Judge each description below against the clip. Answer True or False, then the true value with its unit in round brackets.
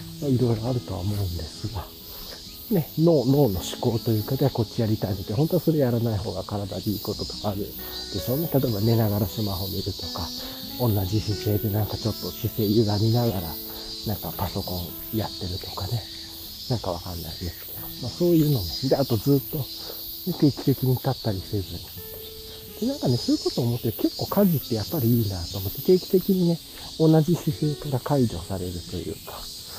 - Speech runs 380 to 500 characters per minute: True (400 characters per minute)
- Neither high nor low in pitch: False (110 Hz)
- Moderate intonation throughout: False (6.1 semitones)